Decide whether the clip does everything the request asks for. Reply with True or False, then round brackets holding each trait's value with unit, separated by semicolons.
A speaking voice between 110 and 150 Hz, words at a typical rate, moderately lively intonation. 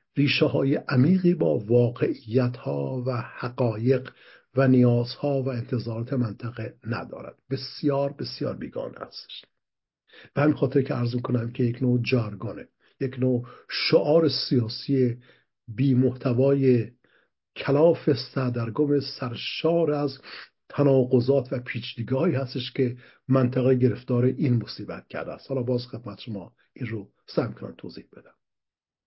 False (130 Hz; 120 wpm; 2.2 semitones)